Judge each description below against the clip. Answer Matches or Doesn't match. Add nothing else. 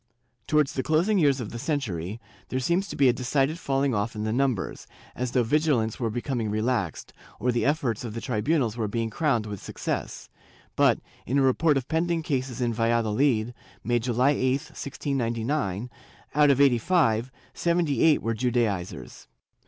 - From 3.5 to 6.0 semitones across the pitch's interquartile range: Matches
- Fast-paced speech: Doesn't match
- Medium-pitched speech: Doesn't match